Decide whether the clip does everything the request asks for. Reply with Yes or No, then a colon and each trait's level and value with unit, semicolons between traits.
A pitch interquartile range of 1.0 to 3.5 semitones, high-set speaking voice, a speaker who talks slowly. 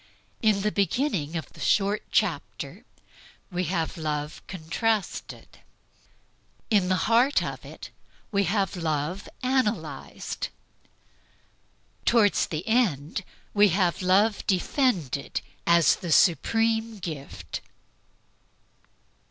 No: average, 4.9 semitones; high, 195 Hz; slow, 95 wpm